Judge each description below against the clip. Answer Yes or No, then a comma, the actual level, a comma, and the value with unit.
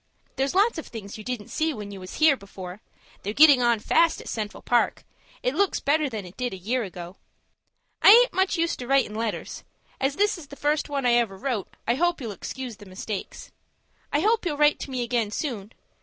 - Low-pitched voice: No, very high, 250 Hz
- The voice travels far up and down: Yes, wide, 6.3 semitones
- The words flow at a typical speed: No, fast, 220 wpm